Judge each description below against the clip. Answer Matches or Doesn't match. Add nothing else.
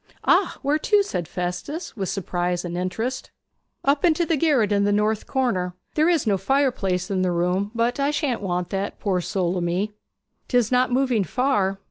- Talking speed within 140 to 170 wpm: Doesn't match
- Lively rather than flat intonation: Matches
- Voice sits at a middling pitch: Doesn't match